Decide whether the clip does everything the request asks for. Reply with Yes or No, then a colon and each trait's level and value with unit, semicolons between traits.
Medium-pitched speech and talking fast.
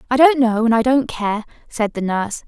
No: high, 235 Hz; fast, 240 wpm